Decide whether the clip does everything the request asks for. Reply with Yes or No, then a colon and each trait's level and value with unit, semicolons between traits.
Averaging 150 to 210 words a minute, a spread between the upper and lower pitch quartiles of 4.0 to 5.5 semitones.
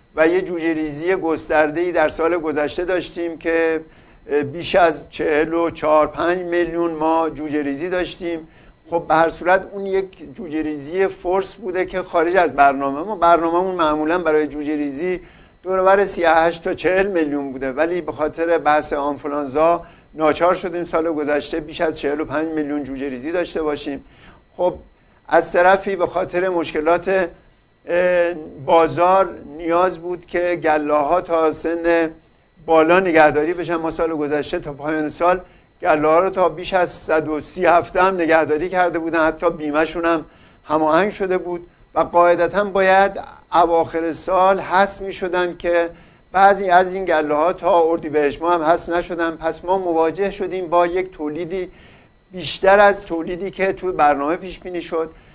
No: fast, 155 wpm; narrow, 2.5 semitones